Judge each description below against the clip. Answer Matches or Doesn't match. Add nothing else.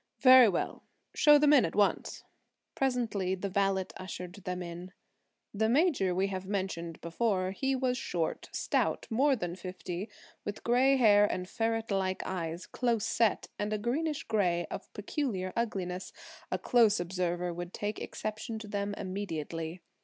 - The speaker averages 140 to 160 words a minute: Matches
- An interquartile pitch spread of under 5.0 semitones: Matches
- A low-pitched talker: Doesn't match